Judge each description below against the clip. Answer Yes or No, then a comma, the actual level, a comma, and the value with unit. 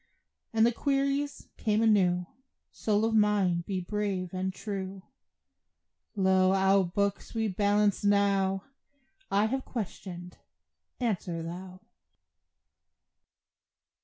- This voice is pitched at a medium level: No, high, 200 Hz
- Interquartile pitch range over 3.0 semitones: No, narrow, 2.4 semitones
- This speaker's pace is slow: Yes, slow, 100 wpm